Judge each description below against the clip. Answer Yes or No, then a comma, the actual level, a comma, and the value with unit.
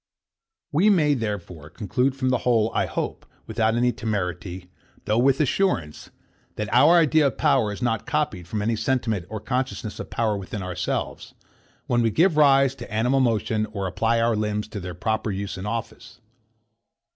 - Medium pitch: No, low, 115 Hz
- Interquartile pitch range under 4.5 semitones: Yes, average, 4.0 semitones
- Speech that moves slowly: No, average, 170 wpm